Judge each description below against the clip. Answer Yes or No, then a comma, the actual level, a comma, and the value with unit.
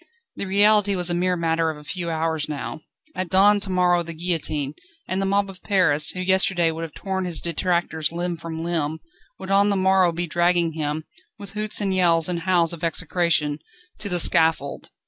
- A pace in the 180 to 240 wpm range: Yes, average, 200 wpm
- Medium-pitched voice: Yes, medium, 175 Hz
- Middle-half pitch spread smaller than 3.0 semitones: Yes, narrow, 2.6 semitones